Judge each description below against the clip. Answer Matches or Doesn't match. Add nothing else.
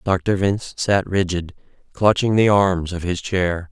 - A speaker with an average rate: Matches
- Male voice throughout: Matches